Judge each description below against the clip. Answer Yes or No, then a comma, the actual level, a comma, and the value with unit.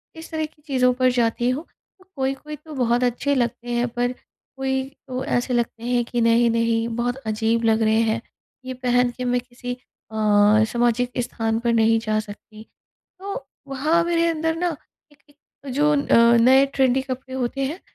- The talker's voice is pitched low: No, high, 245 Hz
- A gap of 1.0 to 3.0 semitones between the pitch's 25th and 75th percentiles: Yes, average, 2.7 semitones